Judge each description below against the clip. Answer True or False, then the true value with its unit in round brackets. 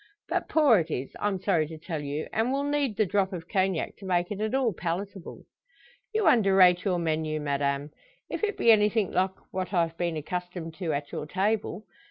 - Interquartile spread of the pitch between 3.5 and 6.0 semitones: True (4.4 semitones)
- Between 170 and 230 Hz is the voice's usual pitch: True (185 Hz)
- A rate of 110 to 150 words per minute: False (200 wpm)